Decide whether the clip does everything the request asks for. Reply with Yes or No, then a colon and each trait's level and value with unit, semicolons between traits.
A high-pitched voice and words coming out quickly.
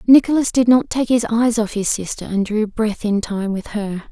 Yes: high, 220 Hz; fast, 235 wpm